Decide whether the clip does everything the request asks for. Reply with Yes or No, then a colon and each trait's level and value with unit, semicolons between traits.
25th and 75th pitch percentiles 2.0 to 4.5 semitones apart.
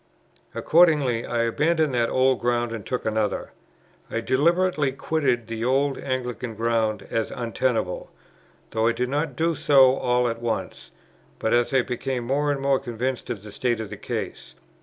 Yes: average, 3.0 semitones